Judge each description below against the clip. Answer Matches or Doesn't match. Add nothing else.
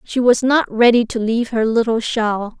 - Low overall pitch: Doesn't match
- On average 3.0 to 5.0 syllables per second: Matches